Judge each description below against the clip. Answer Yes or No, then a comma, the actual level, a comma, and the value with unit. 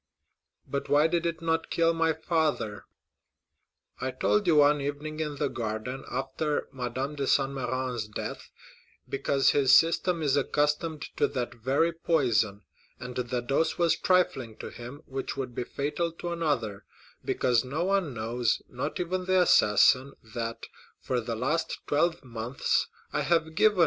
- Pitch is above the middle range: No, medium, 140 Hz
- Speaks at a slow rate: No, average, 155 wpm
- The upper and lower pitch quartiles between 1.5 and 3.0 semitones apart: No, average, 4.8 semitones